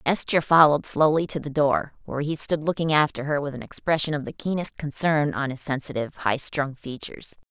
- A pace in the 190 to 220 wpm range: Yes, average, 200 wpm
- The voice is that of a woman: Yes, female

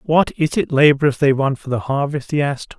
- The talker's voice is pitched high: No, medium, 145 Hz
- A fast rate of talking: Yes, fast, 235 wpm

